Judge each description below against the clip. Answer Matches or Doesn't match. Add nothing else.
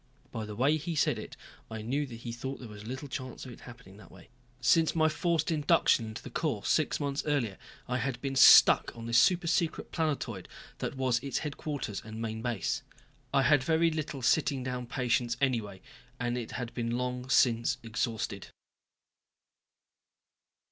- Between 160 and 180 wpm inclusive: Matches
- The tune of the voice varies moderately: Matches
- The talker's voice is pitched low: Matches